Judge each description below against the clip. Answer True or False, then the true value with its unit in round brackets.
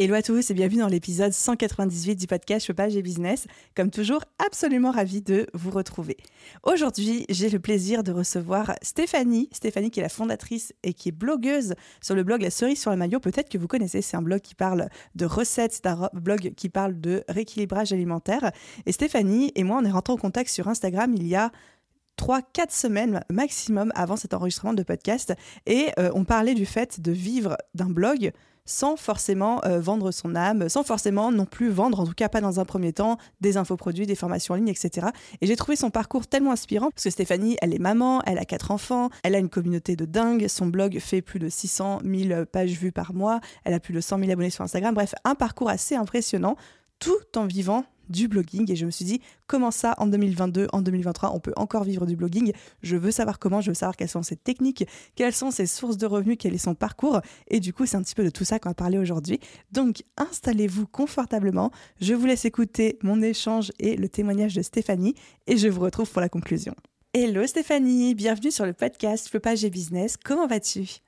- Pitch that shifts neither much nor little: True (3.7 semitones)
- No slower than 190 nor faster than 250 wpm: True (220 wpm)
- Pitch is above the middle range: True (205 Hz)